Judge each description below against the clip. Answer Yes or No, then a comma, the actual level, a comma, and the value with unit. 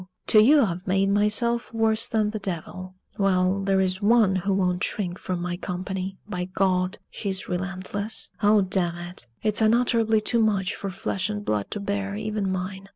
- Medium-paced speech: Yes, average, 175 wpm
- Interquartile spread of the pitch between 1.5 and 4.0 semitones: Yes, narrow, 2.5 semitones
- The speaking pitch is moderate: No, high, 195 Hz